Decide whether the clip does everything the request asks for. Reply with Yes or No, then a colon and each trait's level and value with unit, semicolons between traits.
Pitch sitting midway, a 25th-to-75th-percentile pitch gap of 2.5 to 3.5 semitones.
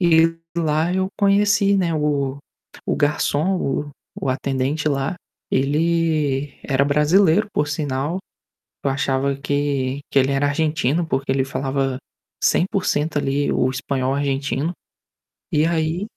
Yes: medium, 145 Hz; average, 3.1 semitones